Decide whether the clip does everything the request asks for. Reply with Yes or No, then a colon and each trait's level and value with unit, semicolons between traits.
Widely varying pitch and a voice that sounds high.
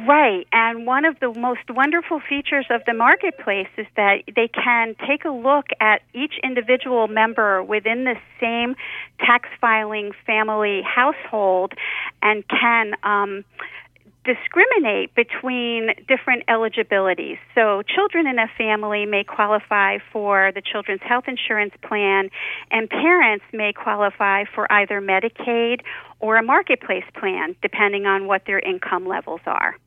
No: average, 3.6 semitones; high, 225 Hz